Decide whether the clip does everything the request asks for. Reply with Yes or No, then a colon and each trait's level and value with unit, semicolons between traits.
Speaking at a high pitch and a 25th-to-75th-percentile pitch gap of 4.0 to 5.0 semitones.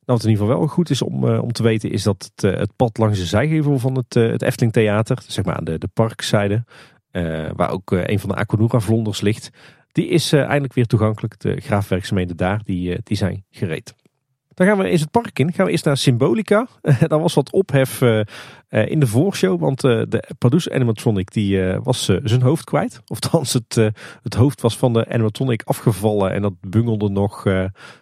No: low, 115 Hz; average, 4.6 semitones